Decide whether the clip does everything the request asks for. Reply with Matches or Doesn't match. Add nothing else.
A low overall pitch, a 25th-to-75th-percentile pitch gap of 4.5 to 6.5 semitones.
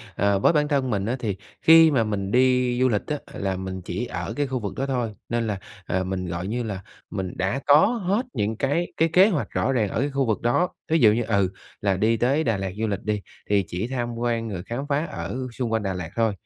Matches